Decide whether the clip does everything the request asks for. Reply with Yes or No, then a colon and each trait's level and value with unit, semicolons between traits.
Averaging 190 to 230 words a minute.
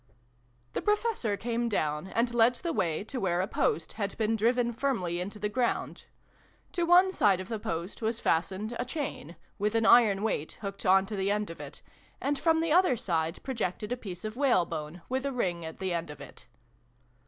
Yes: average, 200 wpm